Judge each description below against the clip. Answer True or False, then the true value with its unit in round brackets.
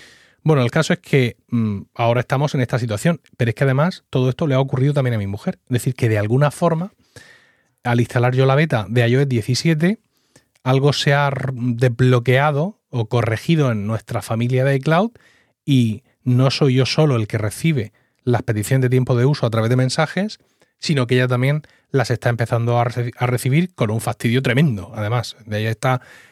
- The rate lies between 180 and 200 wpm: True (190 wpm)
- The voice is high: False (130 Hz)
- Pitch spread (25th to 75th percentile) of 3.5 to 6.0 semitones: False (3.1 semitones)